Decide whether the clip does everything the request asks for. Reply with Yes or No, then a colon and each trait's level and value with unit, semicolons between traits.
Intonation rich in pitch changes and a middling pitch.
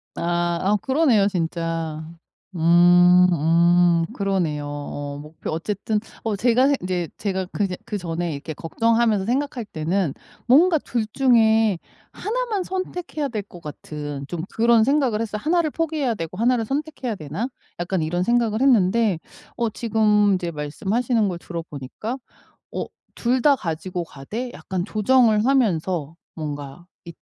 No: wide, 6.1 semitones; high, 200 Hz